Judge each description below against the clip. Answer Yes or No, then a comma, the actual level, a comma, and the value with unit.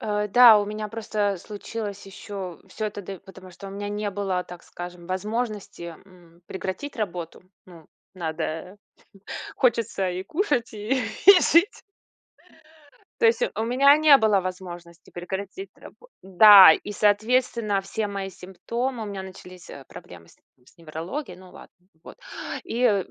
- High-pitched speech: Yes, high, 200 Hz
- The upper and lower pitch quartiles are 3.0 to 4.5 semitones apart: Yes, average, 3.4 semitones